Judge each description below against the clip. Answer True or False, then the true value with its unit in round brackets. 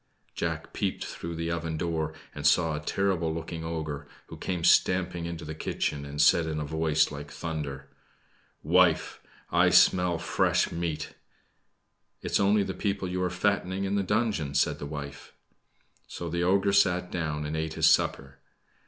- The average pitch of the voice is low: True (85 Hz)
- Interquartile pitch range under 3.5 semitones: True (2.9 semitones)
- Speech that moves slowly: False (170 wpm)